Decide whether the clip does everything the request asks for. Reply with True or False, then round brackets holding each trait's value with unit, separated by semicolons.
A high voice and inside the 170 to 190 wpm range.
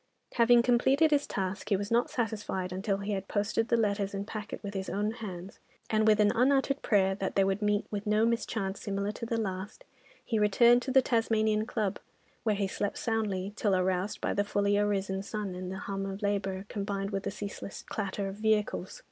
False (205 Hz; 205 wpm)